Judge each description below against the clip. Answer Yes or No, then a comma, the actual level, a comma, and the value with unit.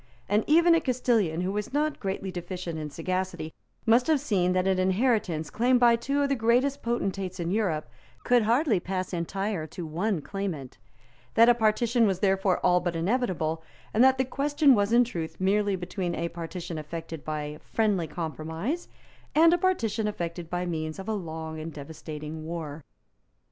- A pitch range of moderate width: No, wide, 6.0 semitones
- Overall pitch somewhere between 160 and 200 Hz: Yes, high, 190 Hz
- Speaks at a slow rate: No, average, 175 wpm